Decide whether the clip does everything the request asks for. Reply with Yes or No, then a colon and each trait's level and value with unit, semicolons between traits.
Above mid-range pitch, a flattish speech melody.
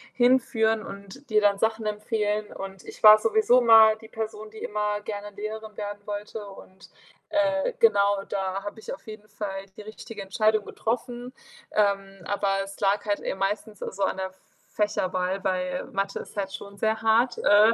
Yes: high, 210 Hz; narrow, 1.9 semitones